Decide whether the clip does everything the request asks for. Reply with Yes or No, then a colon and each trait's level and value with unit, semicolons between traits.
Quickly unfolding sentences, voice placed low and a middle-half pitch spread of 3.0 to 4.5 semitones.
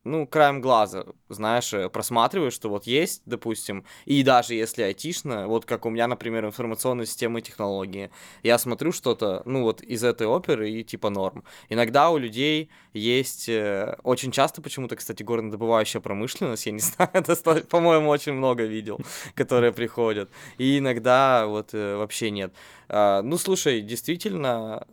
No: average, 145 wpm; low, 120 Hz; average, 4.0 semitones